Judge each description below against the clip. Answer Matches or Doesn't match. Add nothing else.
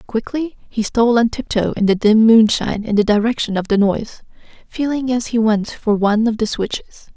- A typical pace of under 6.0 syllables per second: Matches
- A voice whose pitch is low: Doesn't match